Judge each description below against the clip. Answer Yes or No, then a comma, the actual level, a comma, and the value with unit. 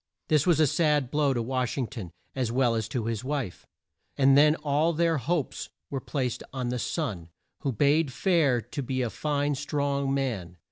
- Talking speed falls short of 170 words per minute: No, average, 190 wpm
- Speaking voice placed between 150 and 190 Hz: No, low, 135 Hz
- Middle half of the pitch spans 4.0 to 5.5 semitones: No, average, 3.4 semitones